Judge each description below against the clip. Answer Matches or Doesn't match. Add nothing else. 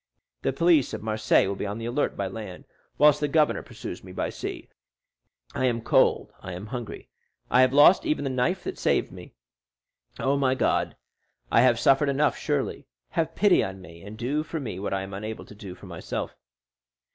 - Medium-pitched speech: Doesn't match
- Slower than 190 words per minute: Doesn't match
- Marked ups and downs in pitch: Matches